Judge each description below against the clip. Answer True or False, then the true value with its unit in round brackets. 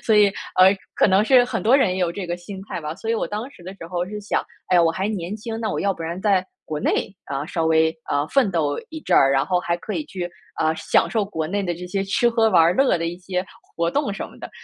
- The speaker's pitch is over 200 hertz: False (185 Hz)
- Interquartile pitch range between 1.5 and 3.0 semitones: False (3.9 semitones)